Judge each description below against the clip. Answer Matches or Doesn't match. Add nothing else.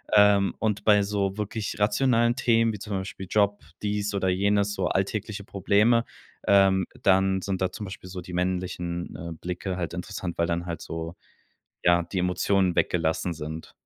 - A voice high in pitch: Doesn't match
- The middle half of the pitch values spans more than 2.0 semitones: Matches